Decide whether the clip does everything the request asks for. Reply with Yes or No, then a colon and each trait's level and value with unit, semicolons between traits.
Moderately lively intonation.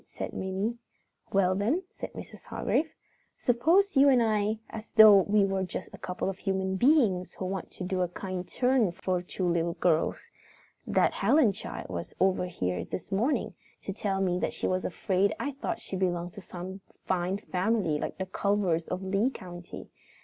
Yes: average, 3.1 semitones